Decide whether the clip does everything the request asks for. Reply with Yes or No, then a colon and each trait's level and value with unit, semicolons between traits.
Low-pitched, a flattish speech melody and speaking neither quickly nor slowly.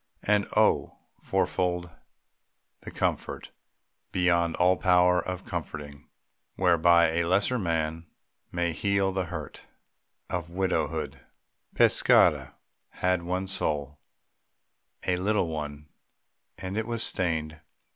No: very low, 90 Hz; narrow, 2.3 semitones; slow, 105 wpm